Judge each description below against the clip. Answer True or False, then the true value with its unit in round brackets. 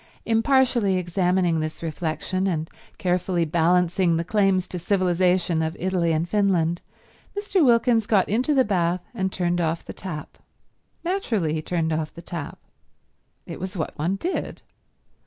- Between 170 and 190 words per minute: False (145 wpm)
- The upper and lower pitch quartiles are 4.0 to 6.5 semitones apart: False (3.0 semitones)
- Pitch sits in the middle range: True (180 Hz)